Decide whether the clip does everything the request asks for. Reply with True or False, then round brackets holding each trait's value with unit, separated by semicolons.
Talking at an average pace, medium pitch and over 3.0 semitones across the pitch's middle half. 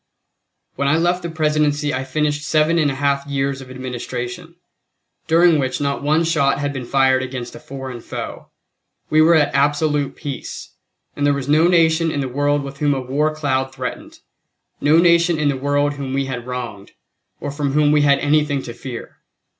False (190 wpm; 145 Hz; 2.4 semitones)